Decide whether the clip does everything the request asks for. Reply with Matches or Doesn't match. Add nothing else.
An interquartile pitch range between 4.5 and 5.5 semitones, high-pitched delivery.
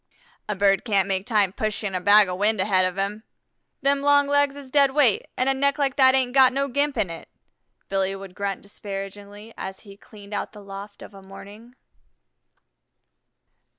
Matches